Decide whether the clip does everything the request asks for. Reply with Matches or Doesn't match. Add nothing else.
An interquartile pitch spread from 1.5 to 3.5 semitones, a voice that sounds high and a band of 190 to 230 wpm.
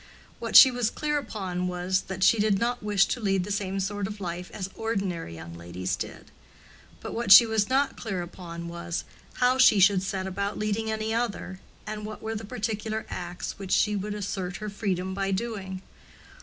Matches